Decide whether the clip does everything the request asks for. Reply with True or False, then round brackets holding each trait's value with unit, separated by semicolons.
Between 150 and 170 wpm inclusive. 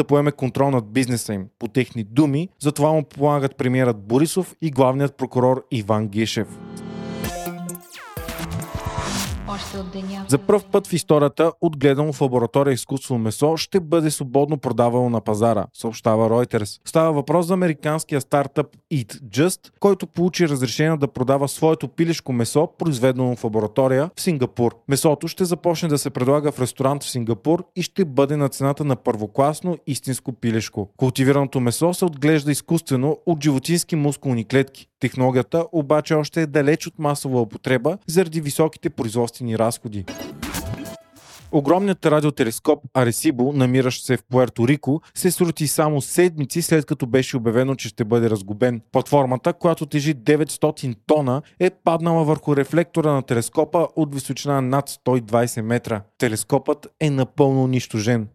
False (140 wpm)